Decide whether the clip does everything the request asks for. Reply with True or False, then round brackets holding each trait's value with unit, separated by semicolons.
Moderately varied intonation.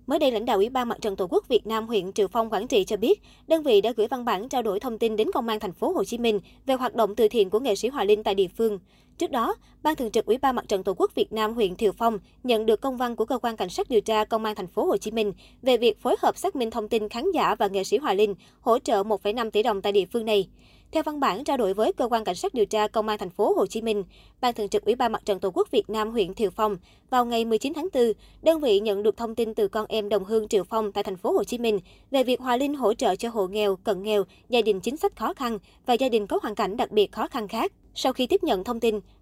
True (4.2 semitones)